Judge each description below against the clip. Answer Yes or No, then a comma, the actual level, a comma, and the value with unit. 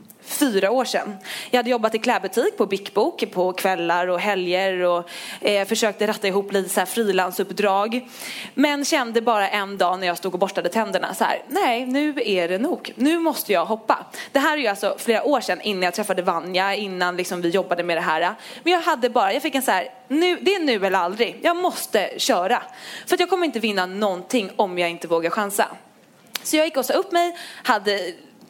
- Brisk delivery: Yes, fast, 215 wpm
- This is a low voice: No, high, 210 Hz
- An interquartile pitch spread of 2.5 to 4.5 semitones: No, wide, 5.6 semitones